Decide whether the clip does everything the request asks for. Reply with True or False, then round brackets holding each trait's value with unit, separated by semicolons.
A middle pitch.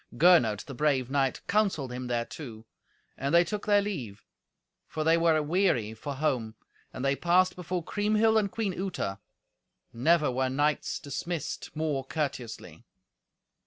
True (150 Hz)